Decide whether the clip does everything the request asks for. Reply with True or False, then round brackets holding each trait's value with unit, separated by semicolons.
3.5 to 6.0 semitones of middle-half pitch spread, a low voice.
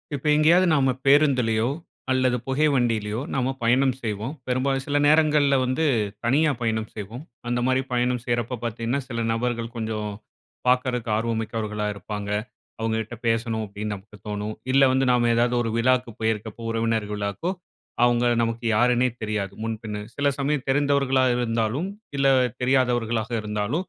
False (2.9 semitones; 120 Hz)